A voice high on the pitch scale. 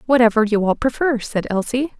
Yes: high, 235 Hz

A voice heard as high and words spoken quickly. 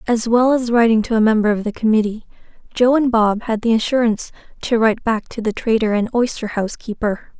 Yes: high, 225 Hz; fast, 210 wpm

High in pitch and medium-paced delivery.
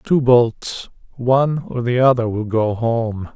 No: low, 120 Hz; average, 160 wpm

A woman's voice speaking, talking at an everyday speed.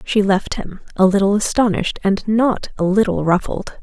Yes: female; average, 170 wpm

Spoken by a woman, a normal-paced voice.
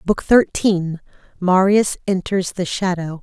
No: female; slow, 95 wpm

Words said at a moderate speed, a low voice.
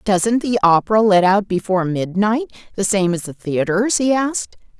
No: average, 175 wpm; high, 200 Hz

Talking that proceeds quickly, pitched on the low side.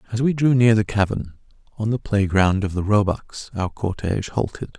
No: average, 190 wpm; low, 105 Hz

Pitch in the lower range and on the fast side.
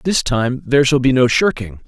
Yes: low, 130 Hz; fast, 225 wpm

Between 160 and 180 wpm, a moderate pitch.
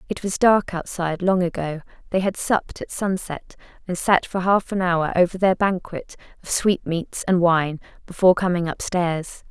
Yes: average, 170 wpm; medium, 180 Hz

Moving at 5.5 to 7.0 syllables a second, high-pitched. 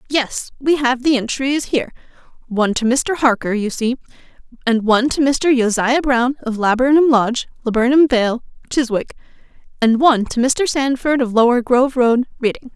No: 5.3 syllables/s; very high, 250 Hz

